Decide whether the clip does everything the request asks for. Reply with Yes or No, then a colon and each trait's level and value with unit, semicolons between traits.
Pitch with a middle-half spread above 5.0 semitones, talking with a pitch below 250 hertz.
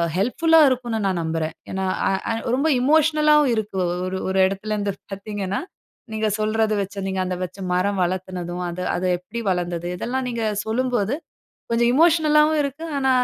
Yes: wide, 5.6 semitones; high, 215 Hz